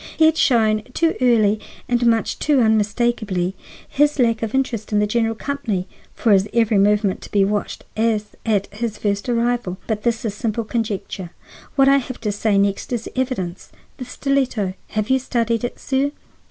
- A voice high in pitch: Yes, high, 225 Hz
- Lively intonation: No, average, 2.9 semitones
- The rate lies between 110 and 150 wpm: No, average, 175 wpm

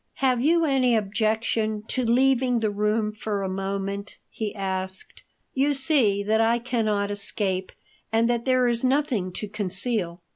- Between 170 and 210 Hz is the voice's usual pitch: No, high, 220 Hz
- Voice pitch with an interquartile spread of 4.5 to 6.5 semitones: No, average, 3.7 semitones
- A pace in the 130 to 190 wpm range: Yes, average, 150 wpm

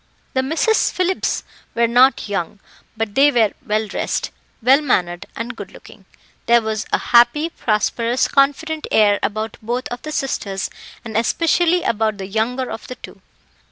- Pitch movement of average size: Yes, average, 4.1 semitones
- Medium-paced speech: Yes, average, 155 wpm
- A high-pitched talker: Yes, high, 235 Hz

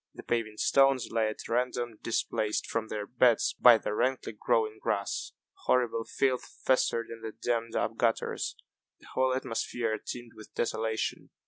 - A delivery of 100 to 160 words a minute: Yes, average, 150 wpm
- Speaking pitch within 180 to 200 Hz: No, low, 115 Hz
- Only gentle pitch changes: Yes, narrow, 2.1 semitones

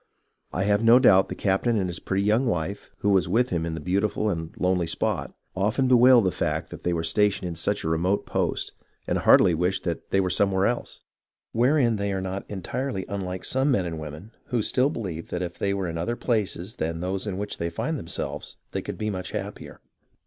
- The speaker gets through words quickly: Yes, fast, 220 wpm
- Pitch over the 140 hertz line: No, very low, 95 Hz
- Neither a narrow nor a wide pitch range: Yes, average, 3.7 semitones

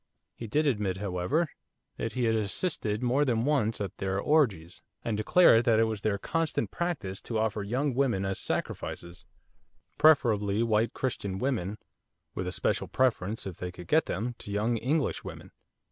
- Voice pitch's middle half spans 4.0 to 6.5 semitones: Yes, average, 4.7 semitones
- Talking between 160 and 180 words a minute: Yes, average, 170 wpm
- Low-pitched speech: Yes, low, 110 Hz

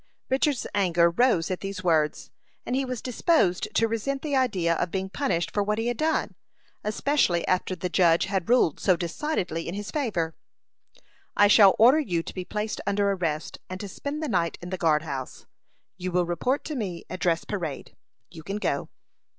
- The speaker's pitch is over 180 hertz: Yes, high, 190 Hz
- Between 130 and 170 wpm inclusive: No, average, 190 wpm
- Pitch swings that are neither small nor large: No, wide, 5.8 semitones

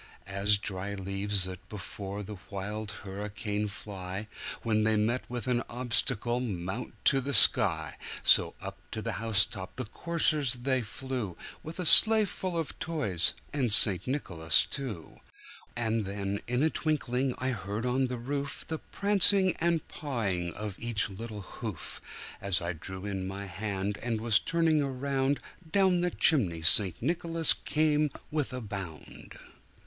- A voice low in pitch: Yes, low, 110 Hz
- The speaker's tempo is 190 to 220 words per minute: No, average, 155 wpm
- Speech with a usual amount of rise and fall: No, wide, 5.8 semitones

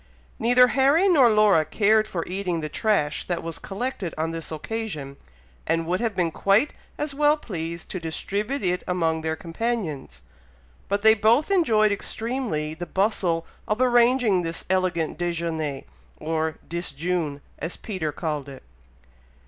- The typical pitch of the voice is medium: Yes, medium, 180 Hz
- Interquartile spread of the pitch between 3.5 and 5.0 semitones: No, wide, 5.6 semitones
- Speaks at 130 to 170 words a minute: Yes, average, 145 wpm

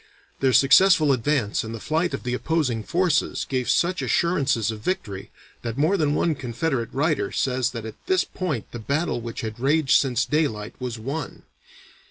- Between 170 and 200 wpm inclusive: Yes, average, 175 wpm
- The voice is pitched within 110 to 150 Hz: Yes, low, 135 Hz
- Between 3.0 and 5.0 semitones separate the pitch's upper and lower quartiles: No, wide, 5.4 semitones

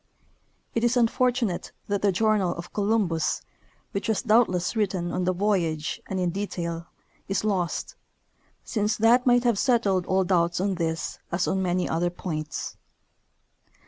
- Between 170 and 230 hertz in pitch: Yes, high, 190 Hz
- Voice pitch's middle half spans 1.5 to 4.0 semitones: Yes, average, 3.7 semitones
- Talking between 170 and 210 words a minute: No, average, 155 wpm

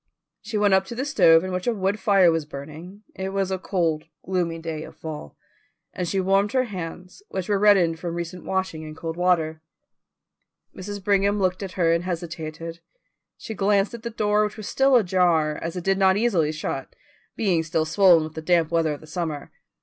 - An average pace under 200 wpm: No, fast, 205 wpm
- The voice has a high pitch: No, medium, 180 Hz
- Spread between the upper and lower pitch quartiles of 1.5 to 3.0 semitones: No, average, 3.4 semitones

